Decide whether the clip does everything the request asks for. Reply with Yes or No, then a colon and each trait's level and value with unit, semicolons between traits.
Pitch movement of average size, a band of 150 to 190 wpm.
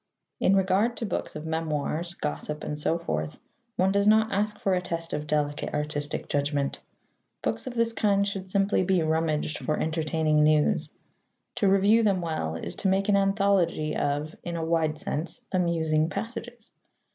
Yes: average, 4.5 semitones; average, 170 wpm